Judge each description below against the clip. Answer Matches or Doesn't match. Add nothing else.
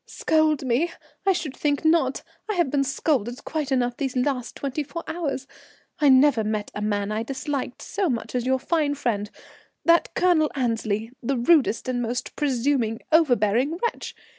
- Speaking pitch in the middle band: Doesn't match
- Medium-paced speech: Matches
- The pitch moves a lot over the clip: Doesn't match